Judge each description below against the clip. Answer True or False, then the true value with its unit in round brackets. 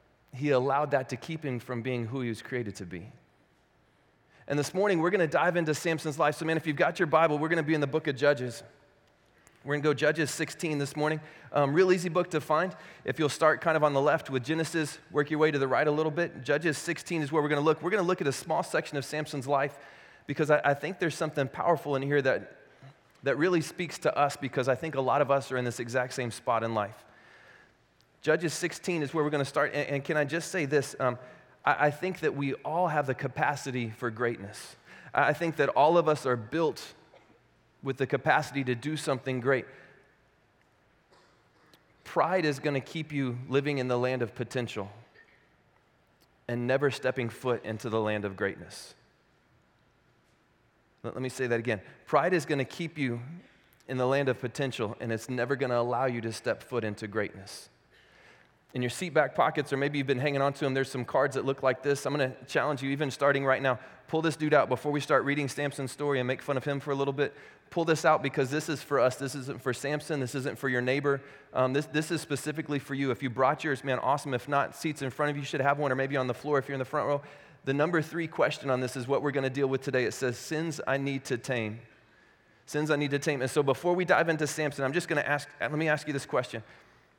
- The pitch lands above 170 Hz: False (140 Hz)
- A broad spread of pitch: False (3.0 semitones)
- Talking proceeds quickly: True (245 wpm)